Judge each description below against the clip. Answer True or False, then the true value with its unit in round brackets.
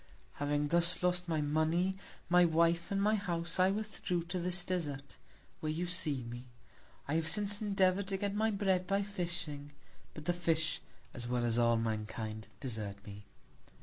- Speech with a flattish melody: False (4.6 semitones)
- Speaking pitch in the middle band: True (170 Hz)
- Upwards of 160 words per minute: True (170 wpm)